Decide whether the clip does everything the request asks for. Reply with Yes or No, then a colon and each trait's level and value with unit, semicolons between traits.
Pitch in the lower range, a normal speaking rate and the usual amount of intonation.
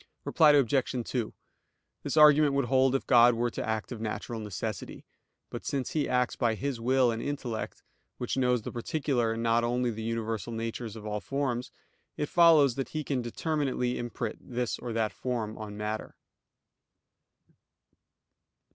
Yes: low, 120 Hz; average, 160 wpm; average, 3.1 semitones